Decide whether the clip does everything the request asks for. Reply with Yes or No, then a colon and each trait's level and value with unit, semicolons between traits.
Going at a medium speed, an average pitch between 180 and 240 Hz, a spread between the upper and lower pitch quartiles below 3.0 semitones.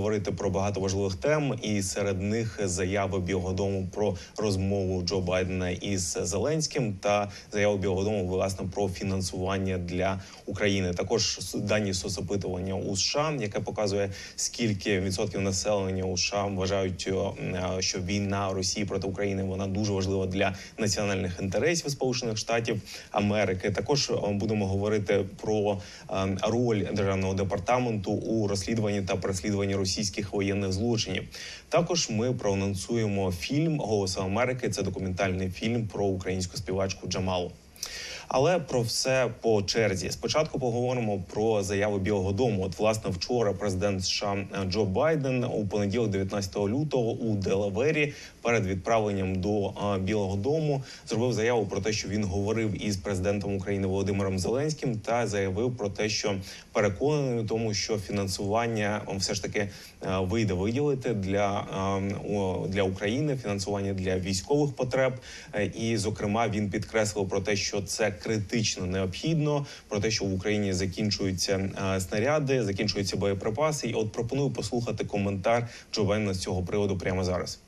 No: average, 135 wpm; low, 100 Hz; narrow, 2.4 semitones